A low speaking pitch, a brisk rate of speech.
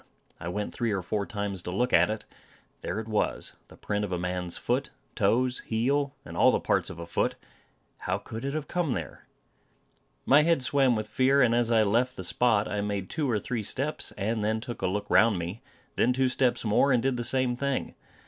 Yes: low, 115 Hz; fast, 220 wpm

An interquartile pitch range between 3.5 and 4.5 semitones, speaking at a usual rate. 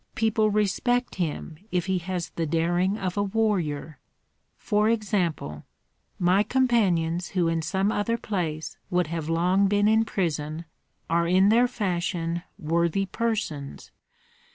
No: average, 4.0 semitones; slow, 130 wpm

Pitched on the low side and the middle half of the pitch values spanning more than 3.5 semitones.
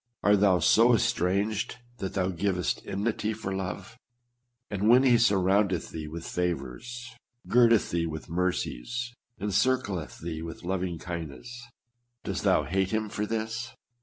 Yes: low, 100 Hz; average, 4.3 semitones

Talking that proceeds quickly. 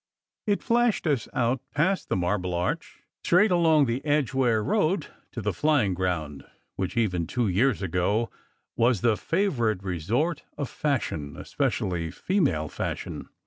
No: average, 140 wpm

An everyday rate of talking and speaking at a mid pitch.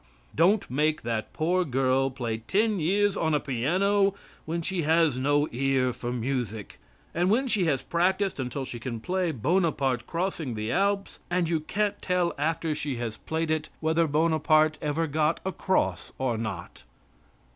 Yes: average, 160 wpm; medium, 155 Hz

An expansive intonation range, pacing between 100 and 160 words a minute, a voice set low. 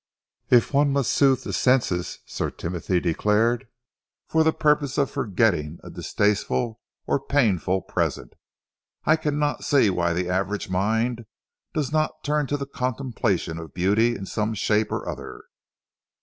Yes: wide, 6.6 semitones; average, 145 wpm; low, 115 Hz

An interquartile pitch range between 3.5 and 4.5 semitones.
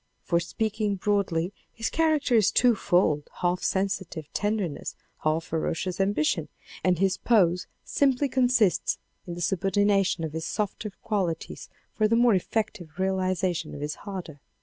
Yes: average, 3.8 semitones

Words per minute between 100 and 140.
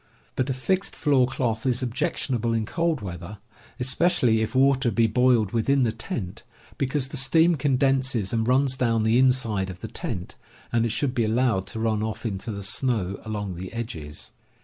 No: average, 180 wpm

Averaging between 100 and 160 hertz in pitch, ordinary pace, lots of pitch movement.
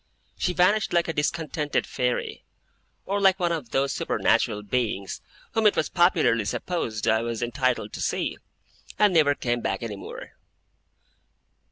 Yes: medium, 140 Hz; average, 150 wpm; wide, 7.1 semitones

